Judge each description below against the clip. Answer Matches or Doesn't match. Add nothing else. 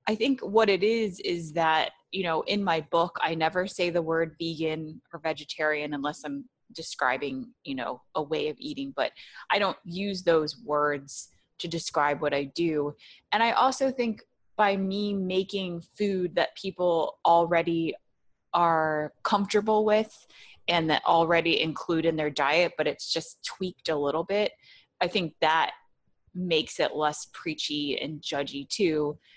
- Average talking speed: Matches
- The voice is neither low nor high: Matches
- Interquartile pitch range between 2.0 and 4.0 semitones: Doesn't match